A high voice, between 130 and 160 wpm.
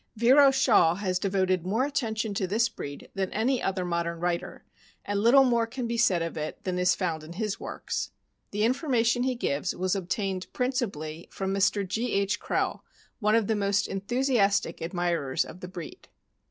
No: high, 200 Hz; average, 180 wpm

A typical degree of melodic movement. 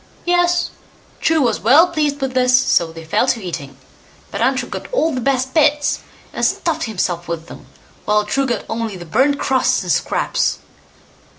No: wide, 6.1 semitones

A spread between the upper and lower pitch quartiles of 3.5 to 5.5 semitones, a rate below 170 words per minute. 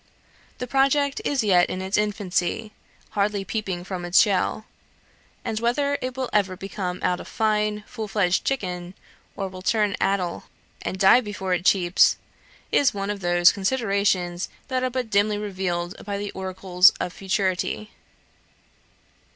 No: average, 2.8 semitones; average, 150 wpm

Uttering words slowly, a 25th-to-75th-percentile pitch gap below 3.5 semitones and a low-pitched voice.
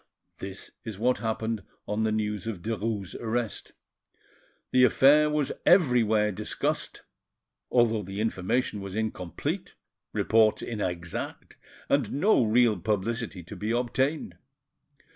Yes: slow, 115 wpm; average, 2.9 semitones; low, 110 Hz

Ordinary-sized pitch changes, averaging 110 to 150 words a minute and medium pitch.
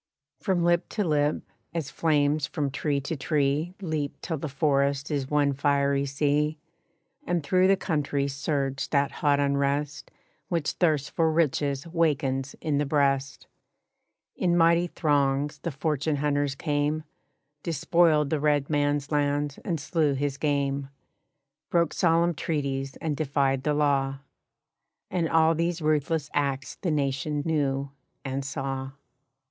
No: narrow, 2.2 semitones; slow, 135 wpm; medium, 145 Hz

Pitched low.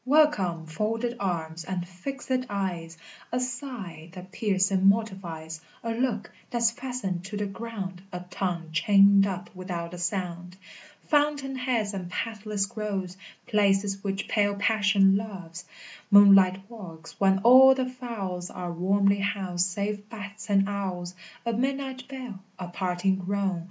No: high, 195 Hz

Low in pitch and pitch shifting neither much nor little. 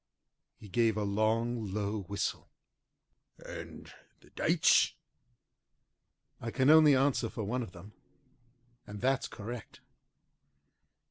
Yes: low, 110 Hz; average, 3.7 semitones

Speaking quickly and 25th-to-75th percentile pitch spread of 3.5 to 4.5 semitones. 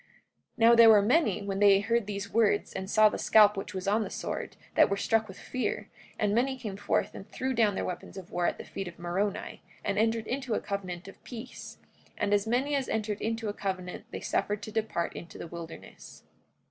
No: fast, 225 wpm; narrow, 2.6 semitones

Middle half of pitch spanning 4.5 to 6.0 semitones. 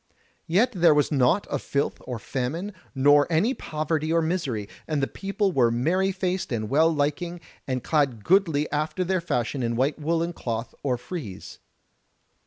Yes: average, 5.1 semitones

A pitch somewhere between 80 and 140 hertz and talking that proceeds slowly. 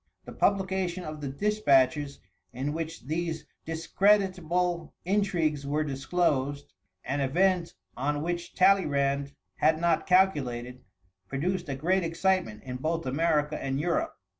No: medium, 160 Hz; slow, 120 wpm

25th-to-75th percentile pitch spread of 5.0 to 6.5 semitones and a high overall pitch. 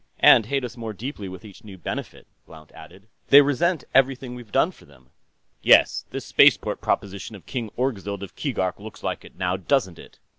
No: average, 5.3 semitones; low, 105 Hz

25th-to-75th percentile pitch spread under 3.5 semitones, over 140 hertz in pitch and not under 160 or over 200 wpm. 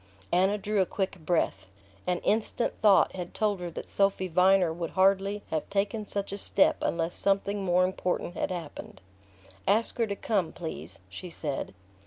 Yes: narrow, 2.6 semitones; high, 190 Hz; average, 170 wpm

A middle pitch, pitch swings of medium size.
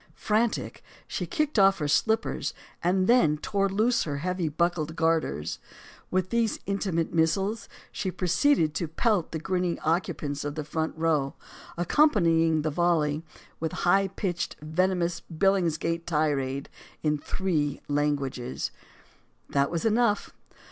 Yes: medium, 170 Hz; average, 4.1 semitones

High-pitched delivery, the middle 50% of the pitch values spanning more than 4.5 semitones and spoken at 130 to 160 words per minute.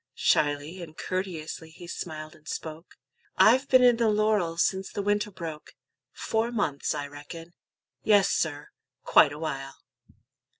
No: medium, 170 Hz; average, 5.1 semitones; average, 140 wpm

